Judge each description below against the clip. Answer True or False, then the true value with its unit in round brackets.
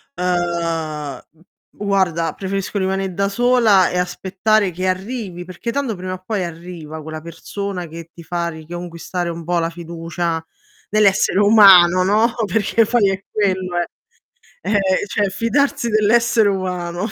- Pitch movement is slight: False (3.1 semitones)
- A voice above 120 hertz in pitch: True (185 Hz)